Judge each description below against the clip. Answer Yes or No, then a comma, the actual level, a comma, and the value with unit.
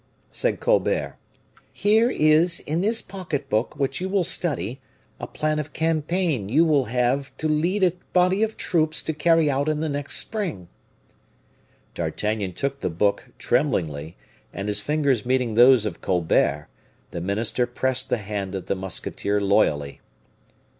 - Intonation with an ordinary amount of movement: No, wide, 7.9 semitones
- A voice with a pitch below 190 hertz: Yes, medium, 140 Hz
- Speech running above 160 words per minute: No, average, 155 wpm